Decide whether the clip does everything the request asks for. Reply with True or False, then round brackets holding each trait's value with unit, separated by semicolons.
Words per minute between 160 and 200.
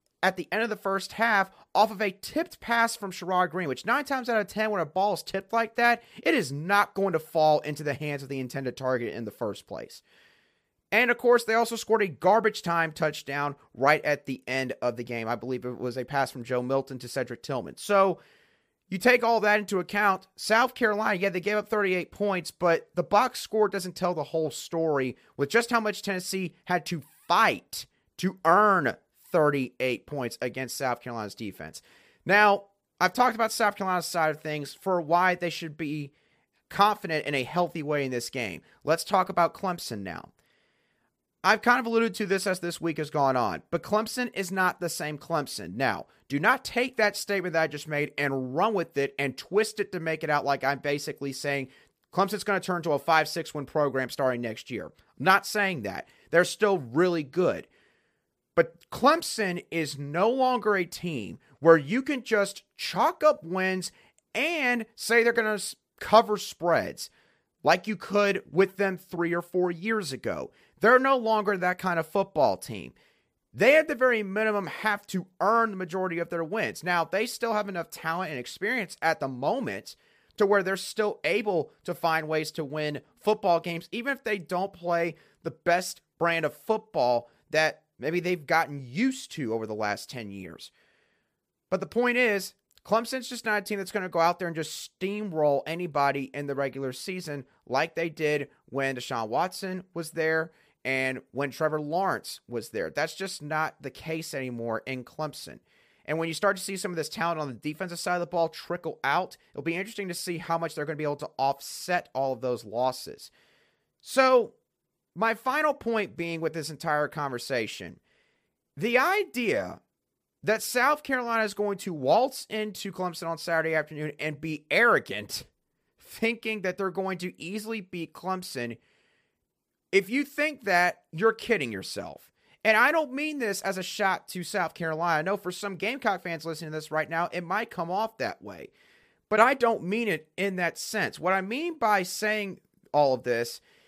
True (195 wpm)